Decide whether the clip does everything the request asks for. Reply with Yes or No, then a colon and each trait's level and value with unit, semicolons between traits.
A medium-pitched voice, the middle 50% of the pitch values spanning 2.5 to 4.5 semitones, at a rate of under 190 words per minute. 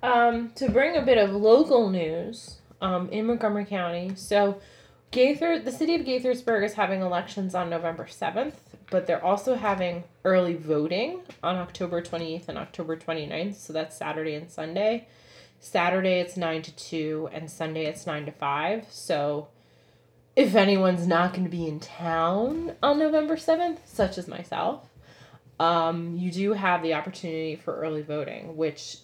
No: medium, 180 Hz; average, 4.9 semitones; average, 160 wpm